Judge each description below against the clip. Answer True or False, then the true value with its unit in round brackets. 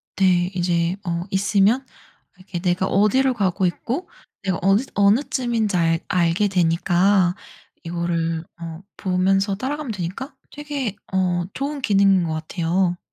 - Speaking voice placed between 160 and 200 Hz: True (190 Hz)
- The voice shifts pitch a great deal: False (3.3 semitones)